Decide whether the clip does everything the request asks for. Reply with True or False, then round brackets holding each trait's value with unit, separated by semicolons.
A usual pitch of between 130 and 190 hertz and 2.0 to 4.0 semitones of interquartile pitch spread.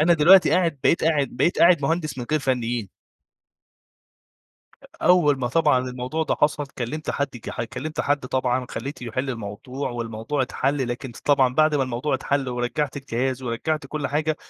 True (135 Hz; 3.6 semitones)